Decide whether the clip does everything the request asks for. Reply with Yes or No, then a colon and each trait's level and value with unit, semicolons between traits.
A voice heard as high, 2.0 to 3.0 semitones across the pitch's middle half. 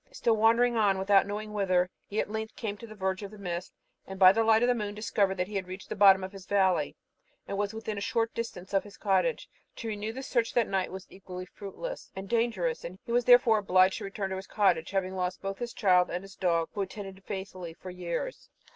Yes: high, 200 Hz; average, 2.7 semitones